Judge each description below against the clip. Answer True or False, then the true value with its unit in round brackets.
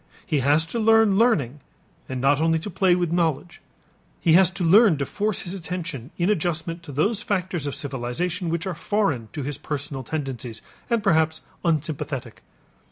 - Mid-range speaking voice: True (165 Hz)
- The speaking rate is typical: True (170 wpm)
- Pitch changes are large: False (4.5 semitones)